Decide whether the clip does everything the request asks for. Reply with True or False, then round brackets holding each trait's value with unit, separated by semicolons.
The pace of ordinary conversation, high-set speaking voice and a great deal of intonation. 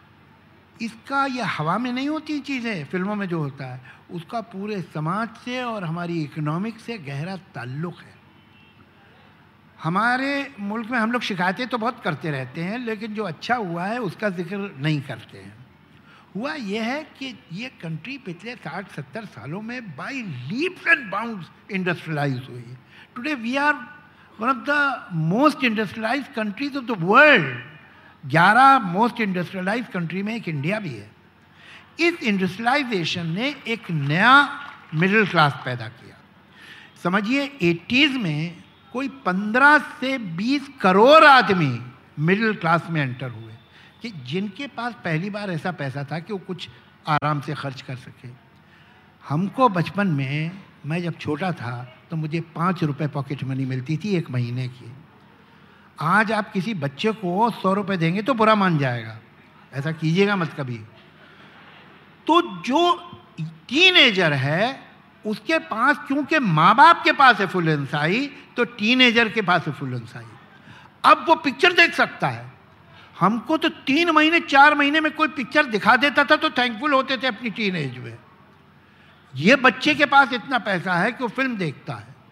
True (155 wpm; 200 Hz; 8.3 semitones)